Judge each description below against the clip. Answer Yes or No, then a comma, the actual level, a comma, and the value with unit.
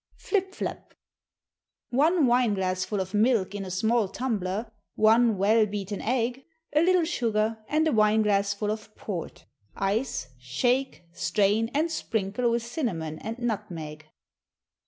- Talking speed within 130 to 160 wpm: Yes, slow, 135 wpm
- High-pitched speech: Yes, high, 215 Hz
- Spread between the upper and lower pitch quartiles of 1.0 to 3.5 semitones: No, average, 3.9 semitones